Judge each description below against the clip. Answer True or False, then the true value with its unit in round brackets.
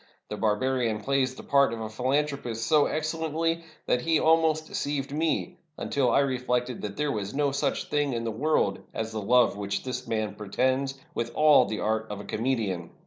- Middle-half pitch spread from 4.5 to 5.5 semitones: True (4.9 semitones)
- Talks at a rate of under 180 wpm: False (190 wpm)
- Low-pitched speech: True (130 Hz)